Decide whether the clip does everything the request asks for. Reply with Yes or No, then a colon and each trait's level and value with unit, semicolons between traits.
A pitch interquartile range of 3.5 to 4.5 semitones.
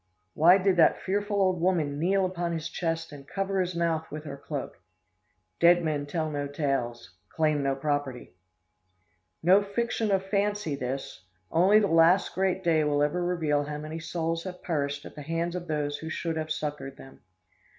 Yes: average, 3.8 semitones